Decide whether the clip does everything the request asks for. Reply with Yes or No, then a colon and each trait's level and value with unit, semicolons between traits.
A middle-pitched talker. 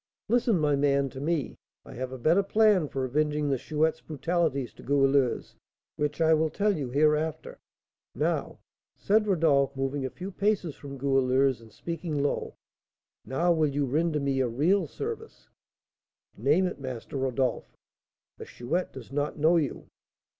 Yes: medium, 150 Hz